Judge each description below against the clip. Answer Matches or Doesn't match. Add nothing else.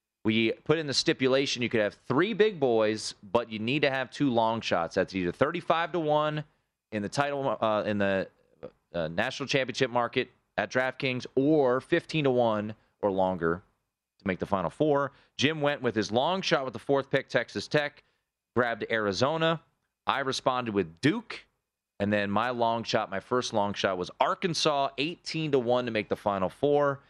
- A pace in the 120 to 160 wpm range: Doesn't match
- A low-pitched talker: Matches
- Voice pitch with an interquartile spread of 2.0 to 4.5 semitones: Doesn't match